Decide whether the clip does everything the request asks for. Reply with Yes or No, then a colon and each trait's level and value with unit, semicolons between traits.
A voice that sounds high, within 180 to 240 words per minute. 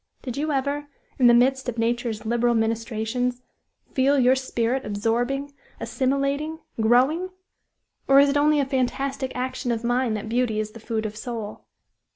No: very high, 250 Hz; average, 160 wpm